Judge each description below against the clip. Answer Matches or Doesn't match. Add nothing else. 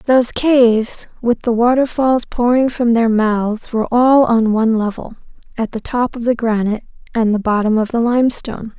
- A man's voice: Doesn't match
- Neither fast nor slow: Matches